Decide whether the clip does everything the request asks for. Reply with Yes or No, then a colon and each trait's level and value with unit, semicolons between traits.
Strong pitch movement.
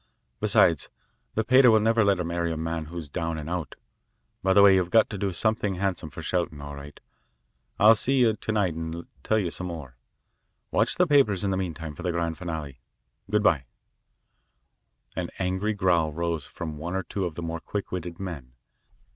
No: average, 3.7 semitones